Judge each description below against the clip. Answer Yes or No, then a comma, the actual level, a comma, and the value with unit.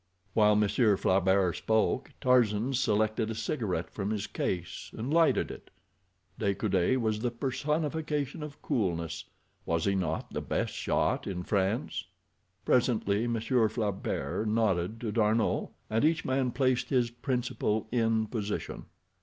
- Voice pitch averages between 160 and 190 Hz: No, low, 110 Hz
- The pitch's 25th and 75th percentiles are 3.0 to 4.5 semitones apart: Yes, average, 3.7 semitones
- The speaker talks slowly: Yes, slow, 130 wpm